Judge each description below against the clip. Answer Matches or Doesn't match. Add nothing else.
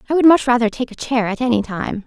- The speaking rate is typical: Doesn't match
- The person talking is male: Doesn't match